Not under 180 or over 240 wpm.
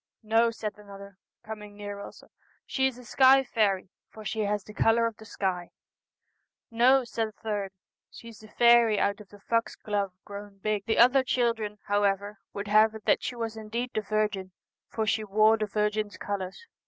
Yes: average, 195 wpm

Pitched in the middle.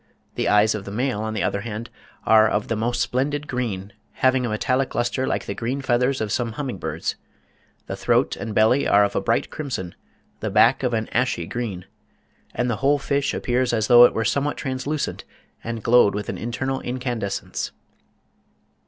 No: low, 120 Hz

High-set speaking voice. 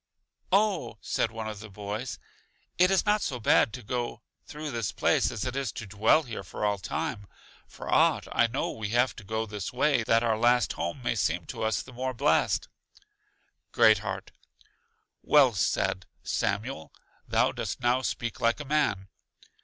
No: low, 115 Hz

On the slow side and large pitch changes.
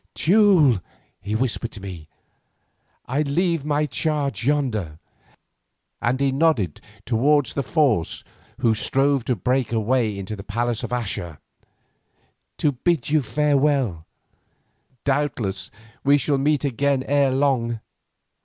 No: slow, 125 wpm; average, 4.6 semitones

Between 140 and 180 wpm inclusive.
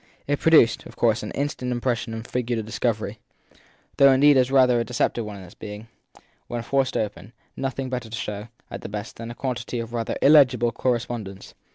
No: average, 200 wpm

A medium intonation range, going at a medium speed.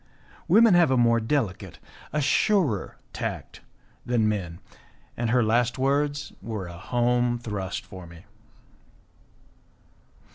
No: average, 5.0 semitones; slow, 115 wpm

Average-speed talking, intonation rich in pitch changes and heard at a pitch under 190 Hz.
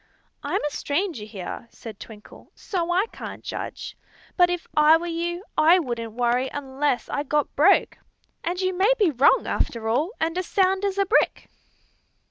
No: average, 170 wpm; wide, 6.3 semitones; very high, 320 Hz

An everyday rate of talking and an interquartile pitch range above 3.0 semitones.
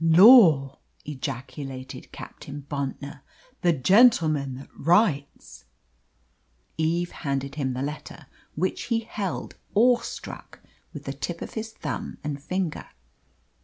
No: slow, 115 wpm; average, 5.1 semitones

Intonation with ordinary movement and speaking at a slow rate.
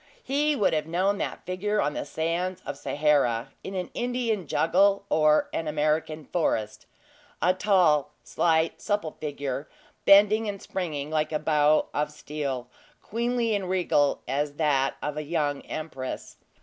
No: average, 4.7 semitones; average, 150 wpm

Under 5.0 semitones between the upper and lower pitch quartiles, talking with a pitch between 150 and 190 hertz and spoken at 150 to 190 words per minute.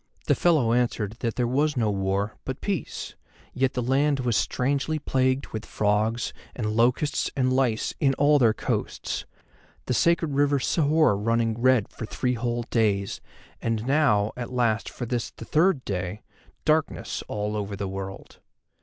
No: average, 4.2 semitones; low, 120 Hz; average, 160 wpm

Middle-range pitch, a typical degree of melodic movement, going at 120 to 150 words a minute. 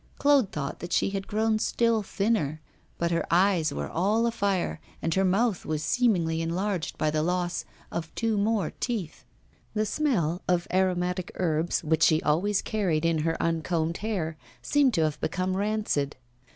No: medium, 180 Hz; average, 4.5 semitones; average, 165 wpm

